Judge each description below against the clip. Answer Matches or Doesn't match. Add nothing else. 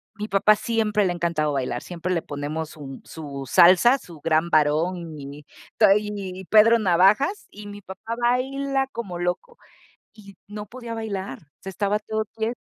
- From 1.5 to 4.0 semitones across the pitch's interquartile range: Doesn't match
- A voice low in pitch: Doesn't match